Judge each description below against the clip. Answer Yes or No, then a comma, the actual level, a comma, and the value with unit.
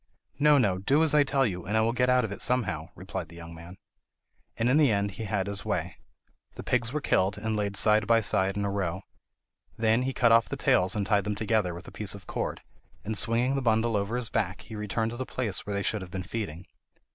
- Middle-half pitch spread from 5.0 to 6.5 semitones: No, average, 3.4 semitones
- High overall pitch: No, low, 105 Hz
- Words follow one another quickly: Yes, fast, 250 wpm